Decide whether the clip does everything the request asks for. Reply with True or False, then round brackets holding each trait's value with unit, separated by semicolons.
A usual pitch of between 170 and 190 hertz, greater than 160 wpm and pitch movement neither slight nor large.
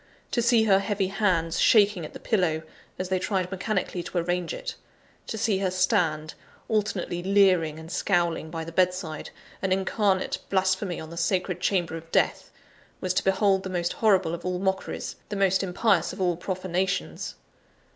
False (185 Hz; 170 wpm; 2.3 semitones)